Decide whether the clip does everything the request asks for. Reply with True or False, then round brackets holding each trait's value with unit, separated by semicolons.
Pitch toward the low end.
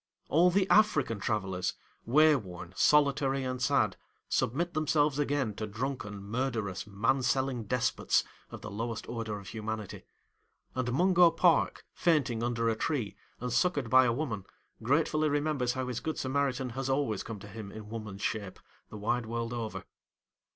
True (125 Hz)